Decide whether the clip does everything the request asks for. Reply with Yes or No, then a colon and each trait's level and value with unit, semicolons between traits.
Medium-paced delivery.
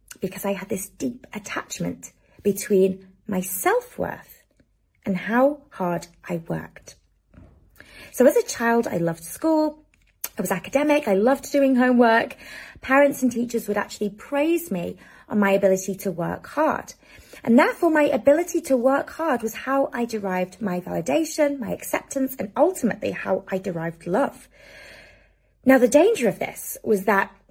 Yes: average, 155 wpm